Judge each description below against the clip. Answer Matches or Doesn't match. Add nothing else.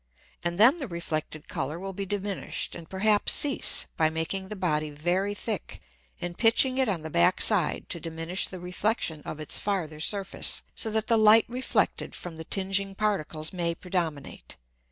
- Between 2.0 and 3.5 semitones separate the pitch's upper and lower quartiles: Doesn't match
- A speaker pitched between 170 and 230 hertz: Matches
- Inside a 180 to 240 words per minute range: Doesn't match